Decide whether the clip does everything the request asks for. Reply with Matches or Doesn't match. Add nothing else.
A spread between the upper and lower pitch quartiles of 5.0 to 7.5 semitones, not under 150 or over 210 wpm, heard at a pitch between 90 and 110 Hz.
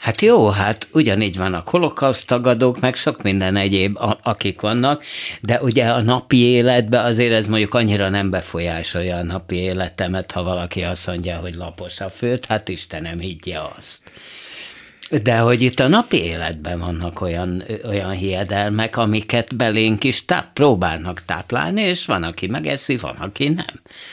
Matches